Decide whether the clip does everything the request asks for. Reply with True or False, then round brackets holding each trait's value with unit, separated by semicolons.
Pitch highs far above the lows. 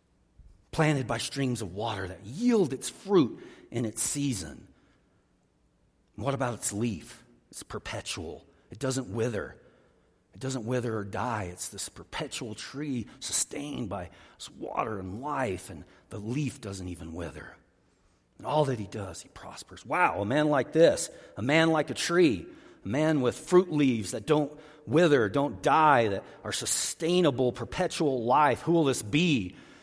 True (6.7 semitones)